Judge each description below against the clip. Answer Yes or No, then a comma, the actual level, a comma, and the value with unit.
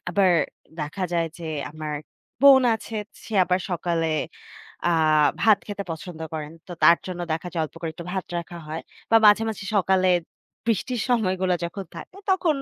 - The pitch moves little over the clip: No, average, 4.0 semitones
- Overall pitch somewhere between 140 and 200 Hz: Yes, medium, 185 Hz